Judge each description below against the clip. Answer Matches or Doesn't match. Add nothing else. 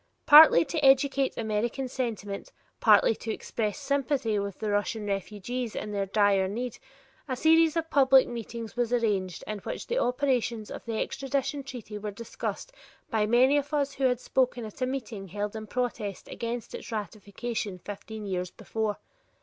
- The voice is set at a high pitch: Matches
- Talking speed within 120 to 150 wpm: Doesn't match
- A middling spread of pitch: Matches